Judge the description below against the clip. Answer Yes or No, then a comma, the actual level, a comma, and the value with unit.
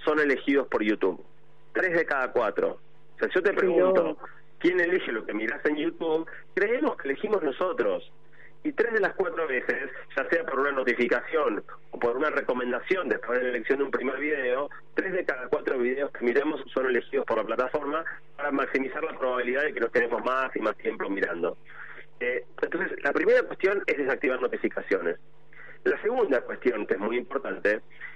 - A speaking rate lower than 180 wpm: No, average, 185 wpm